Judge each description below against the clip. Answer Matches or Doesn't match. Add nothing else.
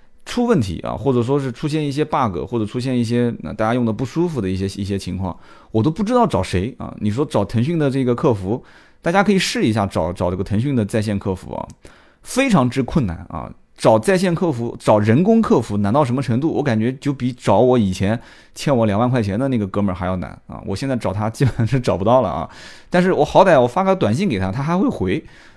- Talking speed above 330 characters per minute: Matches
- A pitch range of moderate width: Doesn't match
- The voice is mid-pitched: Doesn't match